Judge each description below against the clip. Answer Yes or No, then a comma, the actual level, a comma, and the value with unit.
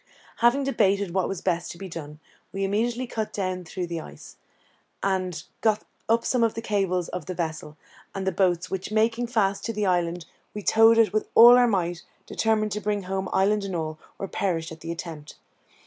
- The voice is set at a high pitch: Yes, high, 195 Hz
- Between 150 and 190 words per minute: No, average, 200 wpm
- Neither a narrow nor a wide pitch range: Yes, average, 3.7 semitones